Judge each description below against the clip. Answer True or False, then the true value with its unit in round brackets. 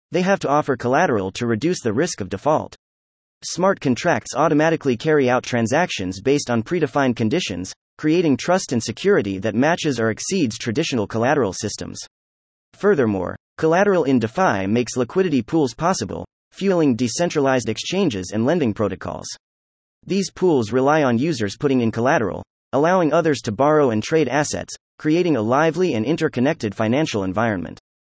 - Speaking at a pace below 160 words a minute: True (145 wpm)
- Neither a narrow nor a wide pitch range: False (6.6 semitones)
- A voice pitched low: True (125 Hz)